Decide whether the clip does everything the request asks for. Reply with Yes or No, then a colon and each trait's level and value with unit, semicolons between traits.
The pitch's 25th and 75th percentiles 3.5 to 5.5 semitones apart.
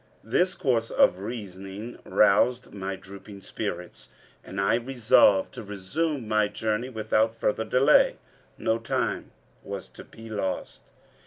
No: average, 3.0 semitones